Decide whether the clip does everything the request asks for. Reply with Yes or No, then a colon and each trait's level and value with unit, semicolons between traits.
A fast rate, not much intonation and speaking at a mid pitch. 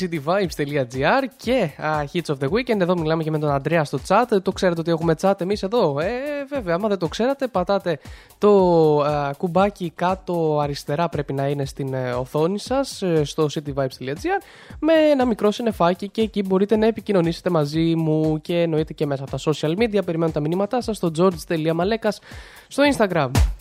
No: fast, 180 wpm; average, 5.1 semitones; medium, 170 Hz